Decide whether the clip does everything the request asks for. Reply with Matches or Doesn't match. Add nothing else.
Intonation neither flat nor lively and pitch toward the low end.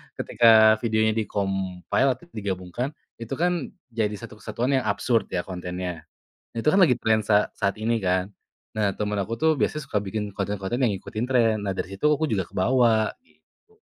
Matches